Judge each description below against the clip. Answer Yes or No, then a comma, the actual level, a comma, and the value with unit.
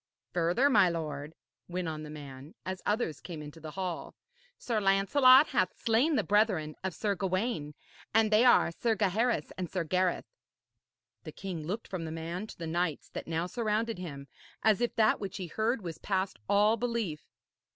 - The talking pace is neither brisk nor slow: Yes, average, 180 wpm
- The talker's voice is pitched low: No, medium, 185 Hz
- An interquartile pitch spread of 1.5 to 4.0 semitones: No, average, 5.0 semitones